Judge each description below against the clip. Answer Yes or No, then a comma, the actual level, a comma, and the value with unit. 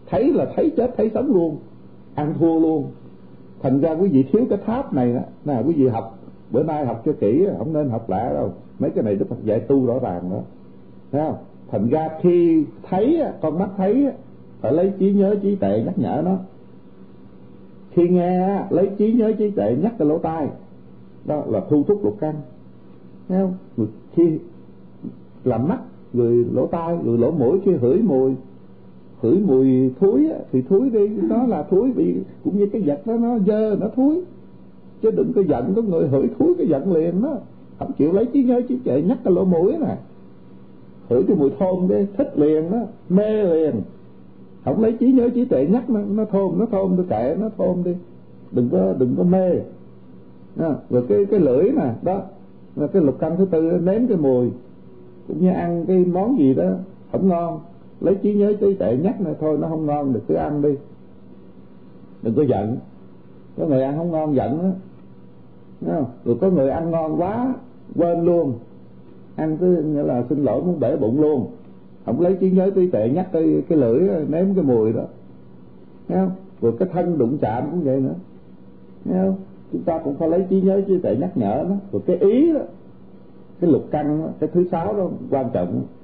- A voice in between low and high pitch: Yes, medium, 160 Hz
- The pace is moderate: Yes, average, 200 wpm